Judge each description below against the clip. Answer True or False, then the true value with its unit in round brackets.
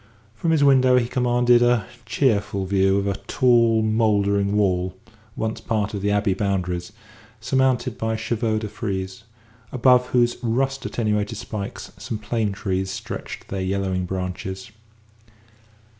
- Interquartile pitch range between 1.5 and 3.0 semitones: False (3.6 semitones)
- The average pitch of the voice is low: True (110 Hz)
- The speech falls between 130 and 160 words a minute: True (135 wpm)